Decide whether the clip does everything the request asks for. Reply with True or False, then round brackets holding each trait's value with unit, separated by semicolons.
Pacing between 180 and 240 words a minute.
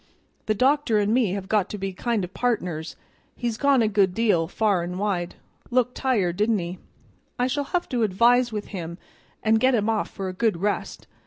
True (200 wpm)